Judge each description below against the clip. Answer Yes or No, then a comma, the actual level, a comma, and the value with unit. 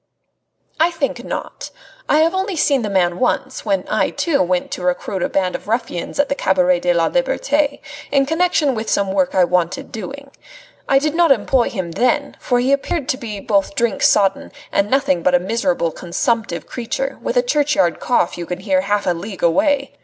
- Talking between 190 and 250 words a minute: Yes, average, 200 wpm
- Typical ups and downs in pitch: No, wide, 7.4 semitones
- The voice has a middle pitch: No, high, 230 Hz